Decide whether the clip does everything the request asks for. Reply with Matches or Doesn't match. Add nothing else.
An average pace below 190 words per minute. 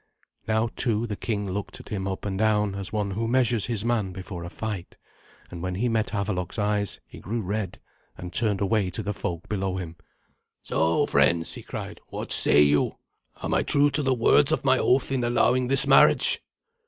Doesn't match